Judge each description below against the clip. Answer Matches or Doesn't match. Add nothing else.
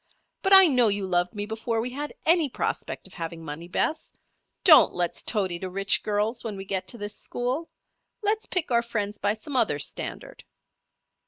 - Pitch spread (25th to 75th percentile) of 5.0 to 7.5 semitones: Matches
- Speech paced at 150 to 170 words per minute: Doesn't match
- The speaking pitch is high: Matches